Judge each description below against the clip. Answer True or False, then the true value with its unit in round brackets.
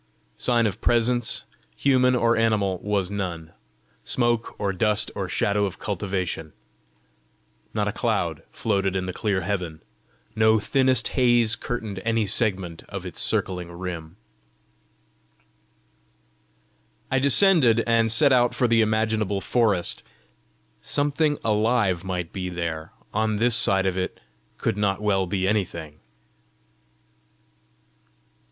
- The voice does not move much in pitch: False (3.9 semitones)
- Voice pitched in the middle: False (105 Hz)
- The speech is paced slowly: True (120 wpm)